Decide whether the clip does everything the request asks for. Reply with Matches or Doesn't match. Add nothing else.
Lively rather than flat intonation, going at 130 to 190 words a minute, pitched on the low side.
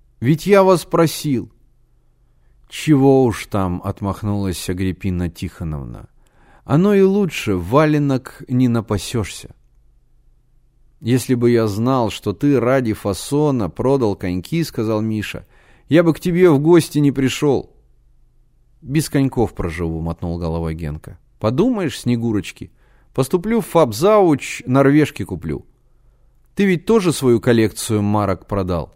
Doesn't match